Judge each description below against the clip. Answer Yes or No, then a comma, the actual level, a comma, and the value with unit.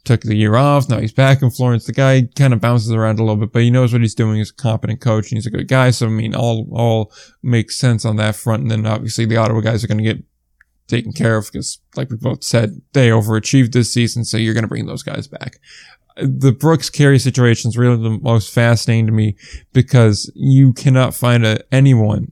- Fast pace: Yes, fast, 240 wpm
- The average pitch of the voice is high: No, low, 115 Hz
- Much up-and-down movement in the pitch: No, narrow, 2.5 semitones